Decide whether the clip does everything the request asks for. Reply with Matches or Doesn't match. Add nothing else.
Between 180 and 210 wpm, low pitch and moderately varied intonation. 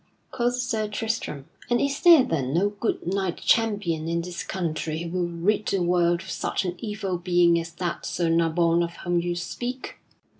Doesn't match